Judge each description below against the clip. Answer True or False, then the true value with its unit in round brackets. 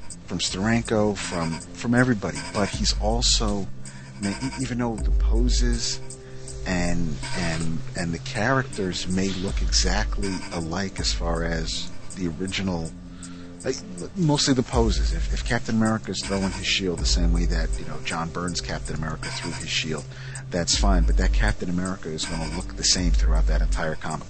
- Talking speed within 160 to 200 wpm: True (165 wpm)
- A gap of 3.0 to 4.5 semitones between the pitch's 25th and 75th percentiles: False (5.0 semitones)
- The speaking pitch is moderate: False (90 Hz)